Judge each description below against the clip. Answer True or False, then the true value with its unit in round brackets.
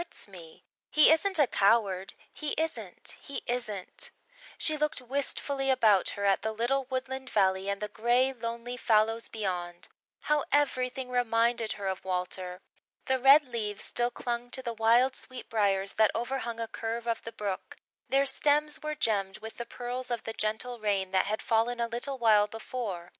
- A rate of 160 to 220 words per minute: True (175 wpm)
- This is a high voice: True (235 Hz)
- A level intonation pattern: False (3.8 semitones)